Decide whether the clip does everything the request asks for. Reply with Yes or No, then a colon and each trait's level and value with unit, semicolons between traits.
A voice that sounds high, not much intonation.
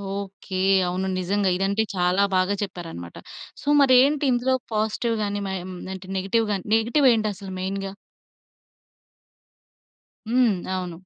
No: high, 200 Hz; average, 3.3 semitones